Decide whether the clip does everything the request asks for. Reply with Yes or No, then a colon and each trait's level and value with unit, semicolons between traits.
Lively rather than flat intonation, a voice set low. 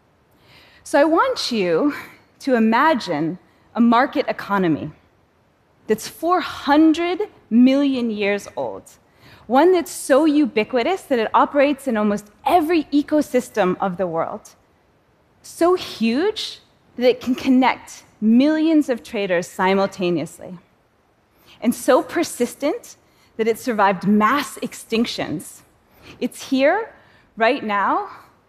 No: wide, 6.0 semitones; very high, 250 Hz